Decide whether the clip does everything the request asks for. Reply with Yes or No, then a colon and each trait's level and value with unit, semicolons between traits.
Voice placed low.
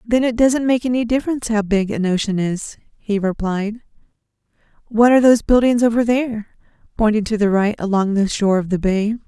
No: high, 220 Hz